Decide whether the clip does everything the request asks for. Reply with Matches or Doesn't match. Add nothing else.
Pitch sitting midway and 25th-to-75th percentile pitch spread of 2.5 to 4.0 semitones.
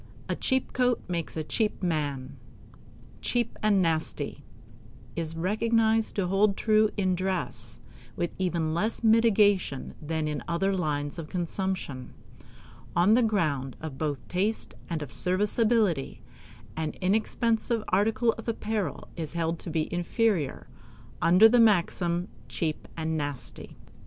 Doesn't match